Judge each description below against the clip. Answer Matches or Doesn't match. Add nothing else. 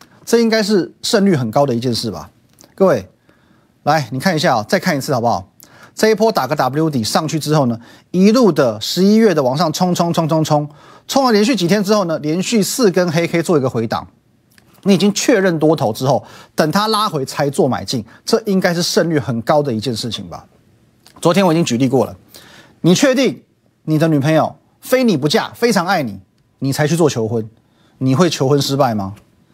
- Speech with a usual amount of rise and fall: Doesn't match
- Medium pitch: Matches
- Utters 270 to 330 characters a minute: Matches